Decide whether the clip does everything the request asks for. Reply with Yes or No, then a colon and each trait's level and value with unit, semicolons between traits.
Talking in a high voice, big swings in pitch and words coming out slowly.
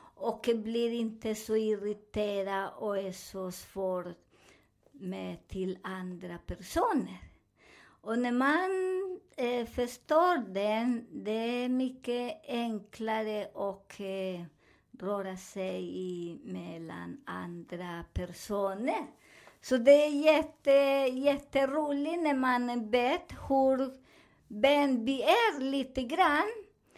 Yes: high, 230 Hz; wide, 5.9 semitones; slow, 100 wpm